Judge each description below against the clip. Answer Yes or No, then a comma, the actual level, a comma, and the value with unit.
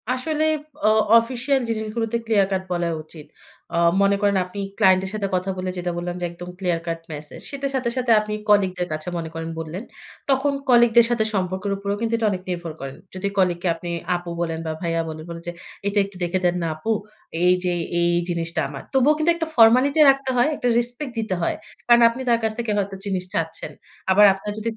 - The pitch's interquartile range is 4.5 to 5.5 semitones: Yes, average, 5.0 semitones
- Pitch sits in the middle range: No, high, 195 Hz